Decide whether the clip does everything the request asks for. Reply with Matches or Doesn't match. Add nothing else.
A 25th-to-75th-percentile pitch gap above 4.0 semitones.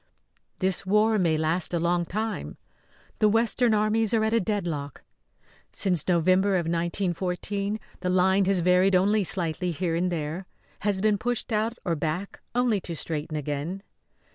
Doesn't match